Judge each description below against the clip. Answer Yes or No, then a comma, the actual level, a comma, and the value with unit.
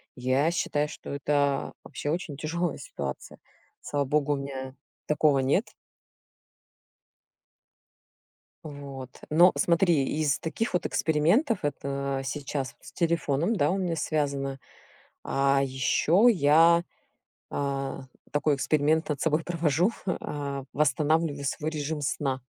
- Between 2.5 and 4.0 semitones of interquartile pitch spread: Yes, average, 2.9 semitones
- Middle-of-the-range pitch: Yes, medium, 150 Hz